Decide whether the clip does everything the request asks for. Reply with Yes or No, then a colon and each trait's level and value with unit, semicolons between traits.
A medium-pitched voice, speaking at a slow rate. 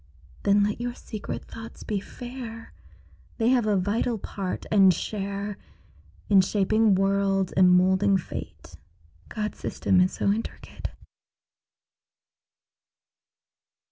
No: high, 200 Hz; slow, 110 wpm